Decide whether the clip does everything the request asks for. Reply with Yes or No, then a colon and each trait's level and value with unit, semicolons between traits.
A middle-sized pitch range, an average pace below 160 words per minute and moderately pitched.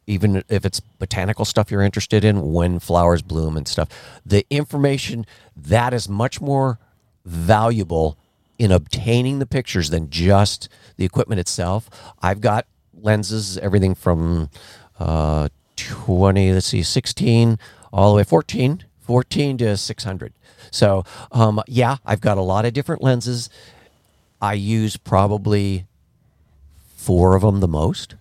No: average, 3.9 semitones; slow, 135 wpm; low, 105 Hz